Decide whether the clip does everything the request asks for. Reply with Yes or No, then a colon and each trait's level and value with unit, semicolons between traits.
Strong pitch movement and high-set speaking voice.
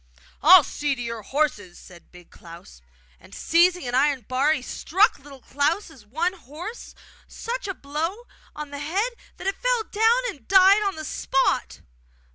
Yes: wide, 6.7 semitones; very high, 300 Hz